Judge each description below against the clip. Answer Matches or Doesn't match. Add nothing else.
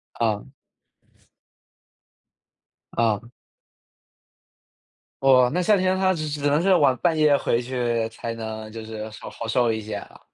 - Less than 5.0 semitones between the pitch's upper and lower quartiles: Doesn't match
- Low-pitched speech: Matches